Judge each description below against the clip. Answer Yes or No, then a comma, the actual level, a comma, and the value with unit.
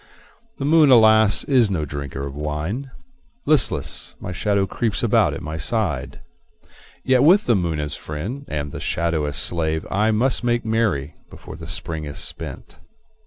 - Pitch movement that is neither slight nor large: No, wide, 7.4 semitones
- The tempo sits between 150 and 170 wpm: Yes, average, 165 wpm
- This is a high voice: No, very low, 90 Hz